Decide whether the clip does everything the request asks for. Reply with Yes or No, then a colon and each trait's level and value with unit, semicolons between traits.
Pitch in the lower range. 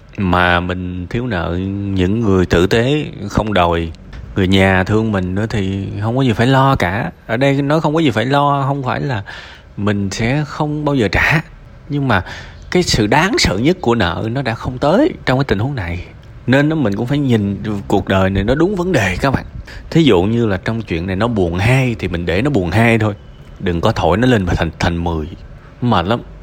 Yes: low, 110 Hz